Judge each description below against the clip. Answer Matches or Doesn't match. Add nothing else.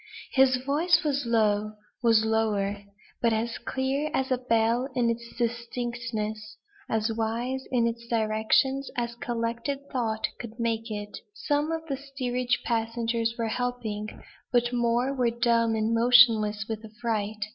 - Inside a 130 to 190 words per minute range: Matches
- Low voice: Doesn't match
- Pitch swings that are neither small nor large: Doesn't match